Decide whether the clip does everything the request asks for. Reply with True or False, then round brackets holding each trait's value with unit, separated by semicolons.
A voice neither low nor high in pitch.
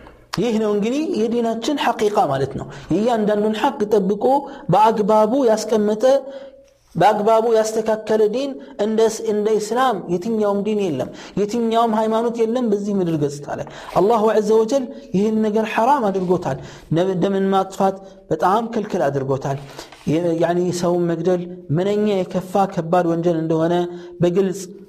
False (210 Hz)